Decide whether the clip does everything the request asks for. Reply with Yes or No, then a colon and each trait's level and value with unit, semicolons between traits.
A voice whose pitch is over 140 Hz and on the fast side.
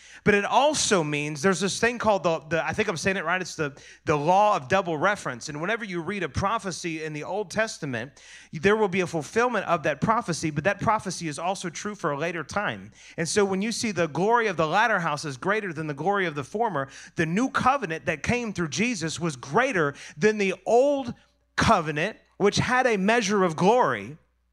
Yes: medium, 185 Hz; fast, 220 wpm